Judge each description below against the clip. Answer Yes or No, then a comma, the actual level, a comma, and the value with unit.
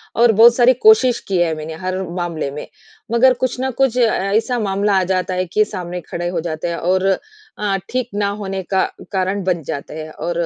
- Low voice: No, high, 190 Hz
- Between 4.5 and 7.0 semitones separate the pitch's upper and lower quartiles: Yes, average, 4.8 semitones